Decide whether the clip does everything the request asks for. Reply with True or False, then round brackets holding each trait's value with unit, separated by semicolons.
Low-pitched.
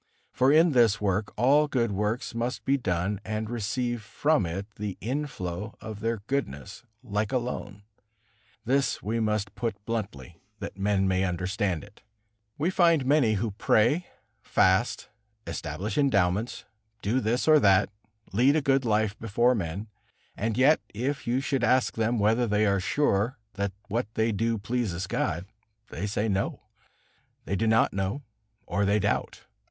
True (110 Hz)